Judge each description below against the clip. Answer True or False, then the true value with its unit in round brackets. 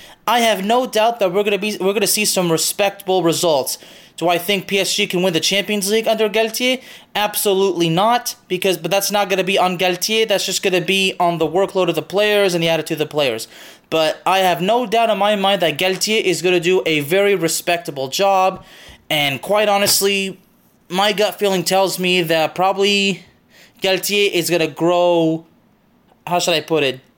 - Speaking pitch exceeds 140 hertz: True (190 Hz)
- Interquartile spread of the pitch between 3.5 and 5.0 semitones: False (2.7 semitones)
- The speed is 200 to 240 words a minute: True (205 wpm)